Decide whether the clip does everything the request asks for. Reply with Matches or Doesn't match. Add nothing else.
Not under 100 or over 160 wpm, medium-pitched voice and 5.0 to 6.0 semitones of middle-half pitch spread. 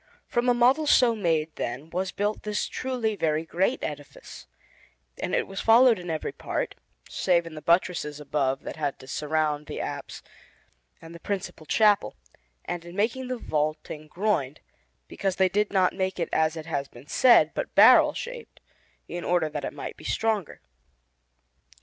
Doesn't match